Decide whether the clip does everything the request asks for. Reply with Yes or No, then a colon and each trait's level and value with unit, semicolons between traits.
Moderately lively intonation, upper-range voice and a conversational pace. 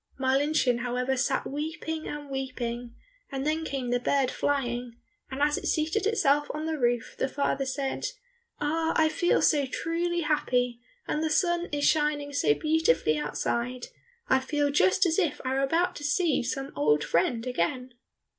Yes: average, 3.8 semitones; very high, 280 Hz; average, 165 wpm